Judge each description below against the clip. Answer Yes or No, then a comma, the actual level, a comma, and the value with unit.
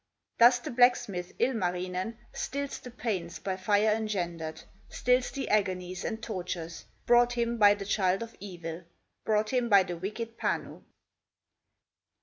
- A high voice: Yes, high, 205 Hz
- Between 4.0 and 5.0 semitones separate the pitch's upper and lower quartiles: Yes, average, 4.4 semitones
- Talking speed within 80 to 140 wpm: Yes, slow, 135 wpm